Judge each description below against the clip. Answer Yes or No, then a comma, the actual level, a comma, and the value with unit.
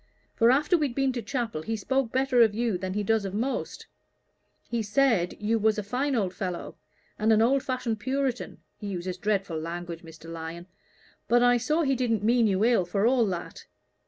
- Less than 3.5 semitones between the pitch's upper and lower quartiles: No, average, 4.9 semitones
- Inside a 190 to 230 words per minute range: Yes, average, 195 wpm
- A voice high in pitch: Yes, high, 225 Hz